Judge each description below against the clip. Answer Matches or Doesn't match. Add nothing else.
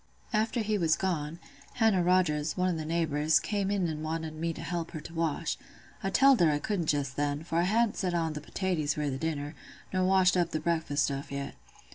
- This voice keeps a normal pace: Doesn't match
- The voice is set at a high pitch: Doesn't match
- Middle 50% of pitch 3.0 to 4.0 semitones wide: Matches